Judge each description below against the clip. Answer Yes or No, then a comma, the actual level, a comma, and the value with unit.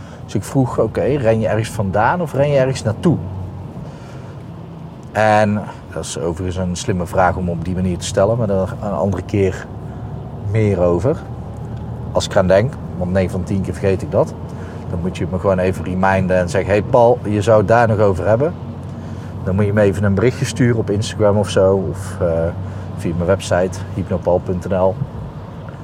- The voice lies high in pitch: No, low, 100 Hz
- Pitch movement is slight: No, average, 3.7 semitones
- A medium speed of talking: Yes, average, 190 wpm